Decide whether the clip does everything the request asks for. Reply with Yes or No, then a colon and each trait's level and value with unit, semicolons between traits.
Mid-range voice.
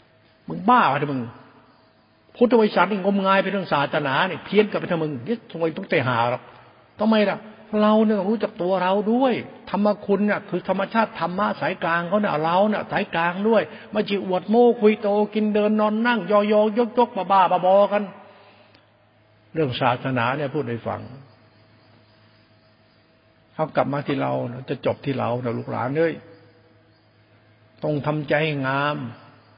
Yes: medium, 165 Hz